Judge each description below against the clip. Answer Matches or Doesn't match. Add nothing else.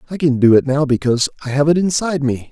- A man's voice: Matches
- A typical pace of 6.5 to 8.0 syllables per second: Matches